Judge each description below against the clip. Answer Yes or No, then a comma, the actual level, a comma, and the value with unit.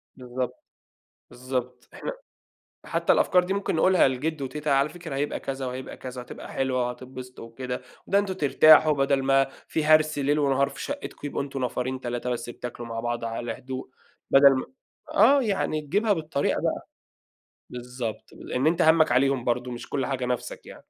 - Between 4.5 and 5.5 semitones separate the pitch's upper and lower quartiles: No, average, 3.5 semitones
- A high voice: No, low, 135 Hz